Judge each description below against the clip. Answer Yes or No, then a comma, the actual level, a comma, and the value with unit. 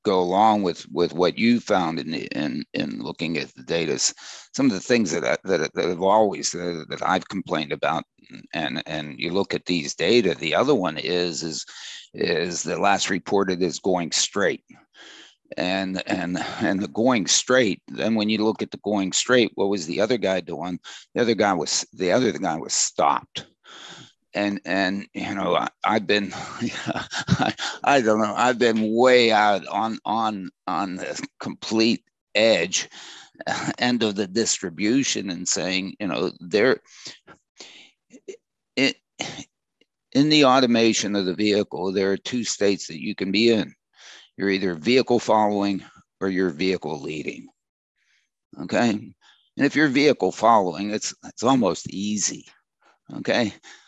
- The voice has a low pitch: Yes, low, 100 Hz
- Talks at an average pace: Yes, average, 160 wpm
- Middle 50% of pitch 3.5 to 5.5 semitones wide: No, average, 3.1 semitones